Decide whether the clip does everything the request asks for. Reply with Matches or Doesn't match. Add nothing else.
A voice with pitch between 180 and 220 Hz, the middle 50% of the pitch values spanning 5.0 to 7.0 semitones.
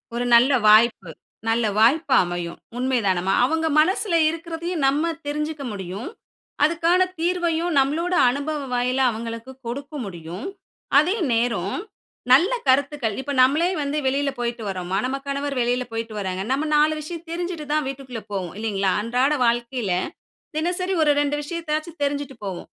Doesn't match